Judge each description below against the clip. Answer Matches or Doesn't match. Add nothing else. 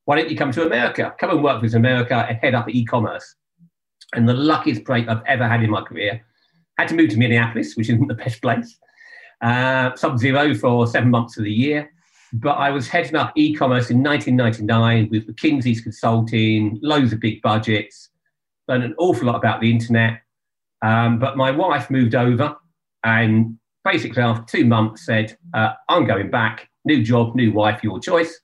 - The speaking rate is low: Doesn't match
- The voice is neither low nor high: Doesn't match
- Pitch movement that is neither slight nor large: Matches